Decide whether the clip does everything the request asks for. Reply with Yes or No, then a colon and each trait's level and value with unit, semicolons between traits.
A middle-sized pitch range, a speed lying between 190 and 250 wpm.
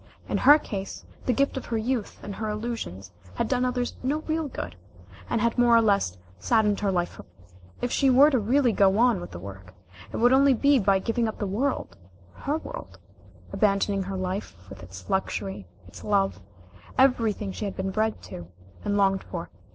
Yes: average, 4.4 semitones; average, 195 wpm